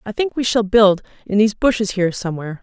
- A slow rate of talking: No, fast, 230 wpm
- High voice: Yes, high, 210 Hz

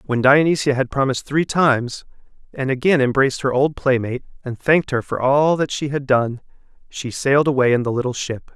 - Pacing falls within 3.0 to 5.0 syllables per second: No, 5.8 syllables/s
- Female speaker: No, male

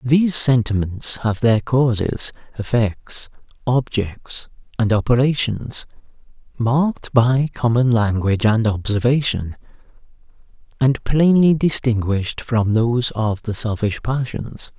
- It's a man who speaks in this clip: Yes, male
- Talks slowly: Yes, slow, 95 wpm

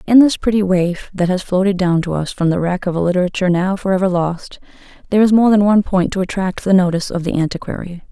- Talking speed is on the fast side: Yes, fast, 235 wpm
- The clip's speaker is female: Yes, female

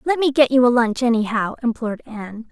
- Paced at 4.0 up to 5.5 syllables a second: No, 6.1 syllables/s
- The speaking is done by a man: No, female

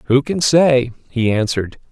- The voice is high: No, low, 130 Hz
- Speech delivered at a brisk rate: No, average, 155 wpm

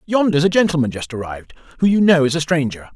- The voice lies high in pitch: No, medium, 155 Hz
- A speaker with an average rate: No, fast, 225 wpm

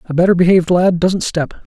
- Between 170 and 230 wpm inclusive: Yes, fast, 205 wpm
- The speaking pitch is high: No, medium, 175 Hz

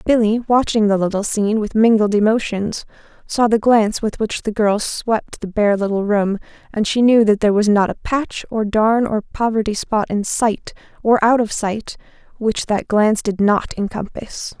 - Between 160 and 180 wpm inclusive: No, average, 190 wpm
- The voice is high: Yes, high, 215 Hz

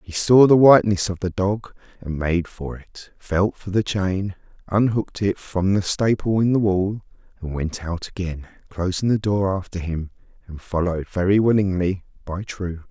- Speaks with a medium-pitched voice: No, very low, 95 Hz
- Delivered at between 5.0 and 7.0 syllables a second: No, 4.7 syllables/s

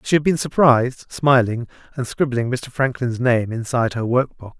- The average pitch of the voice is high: No, low, 125 Hz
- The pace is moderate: Yes, average, 170 wpm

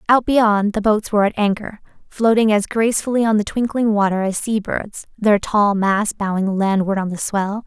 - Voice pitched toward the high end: Yes, high, 210 Hz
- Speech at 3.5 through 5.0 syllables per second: Yes, 4.9 syllables/s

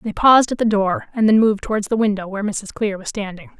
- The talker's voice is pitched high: Yes, high, 210 Hz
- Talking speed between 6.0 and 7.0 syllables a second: Yes, 6.5 syllables/s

